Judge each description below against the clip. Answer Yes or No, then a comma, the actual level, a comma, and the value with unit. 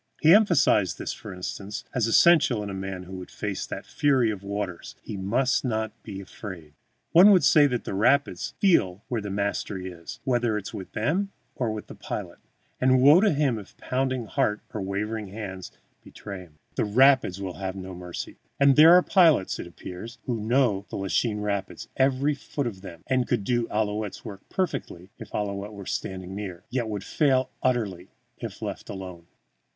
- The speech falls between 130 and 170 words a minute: No, average, 185 wpm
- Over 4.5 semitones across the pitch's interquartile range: Yes, average, 5.2 semitones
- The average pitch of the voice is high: No, low, 105 Hz